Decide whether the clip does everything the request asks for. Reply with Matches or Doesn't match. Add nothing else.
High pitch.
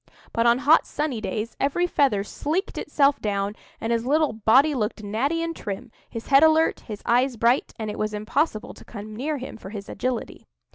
Matches